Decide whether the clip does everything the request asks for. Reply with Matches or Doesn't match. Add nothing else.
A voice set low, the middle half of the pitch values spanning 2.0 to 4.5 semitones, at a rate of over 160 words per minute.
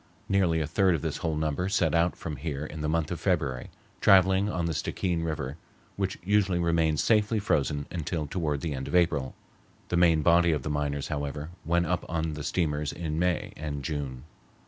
Matches